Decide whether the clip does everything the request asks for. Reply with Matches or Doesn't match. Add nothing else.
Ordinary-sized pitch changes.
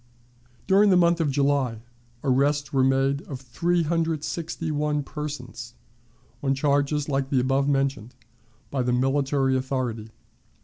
Doesn't match